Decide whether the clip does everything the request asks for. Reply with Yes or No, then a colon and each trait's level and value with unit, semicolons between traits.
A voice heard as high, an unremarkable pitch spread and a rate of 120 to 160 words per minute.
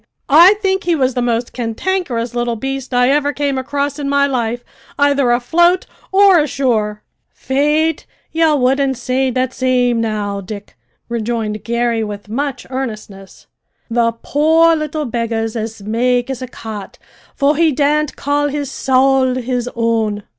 Yes: very high, 255 Hz; average, 3.8 semitones; average, 145 wpm